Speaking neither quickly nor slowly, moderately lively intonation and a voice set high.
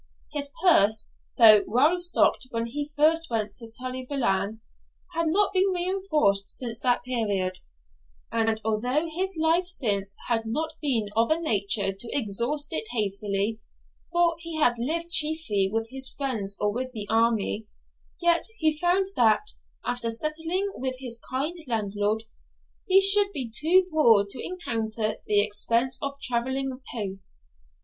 No: average, 145 wpm; wide, 6.6 semitones; very high, 250 Hz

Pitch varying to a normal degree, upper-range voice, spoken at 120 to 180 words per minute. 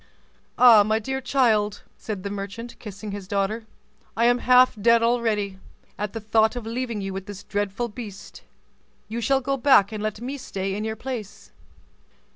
Yes: average, 3.0 semitones; high, 220 Hz; average, 175 wpm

